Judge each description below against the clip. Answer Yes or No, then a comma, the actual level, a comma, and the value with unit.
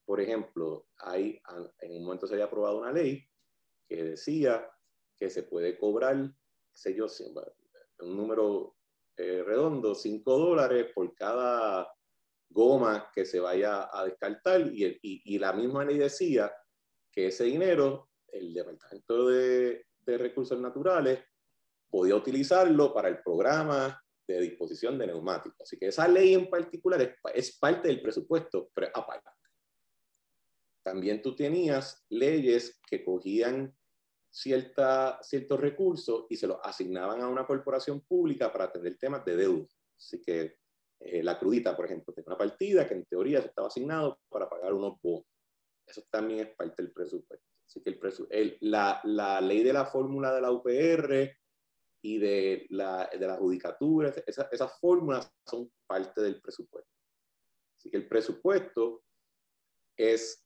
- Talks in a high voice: No, low, 135 Hz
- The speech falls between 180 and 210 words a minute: No, average, 150 wpm